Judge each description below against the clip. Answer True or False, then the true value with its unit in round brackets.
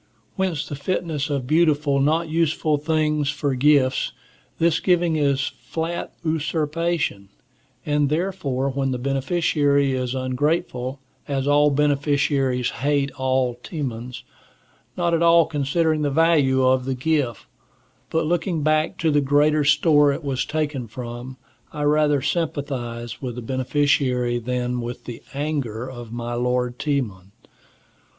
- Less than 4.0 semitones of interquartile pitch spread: True (3.2 semitones)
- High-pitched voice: False (145 Hz)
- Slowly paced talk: True (130 wpm)